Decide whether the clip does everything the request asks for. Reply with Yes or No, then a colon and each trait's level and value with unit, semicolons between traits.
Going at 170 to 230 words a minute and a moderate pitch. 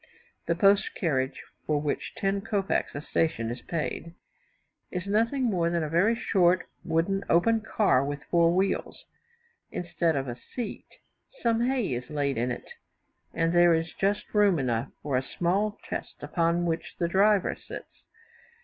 No: average, 160 wpm; medium, 170 Hz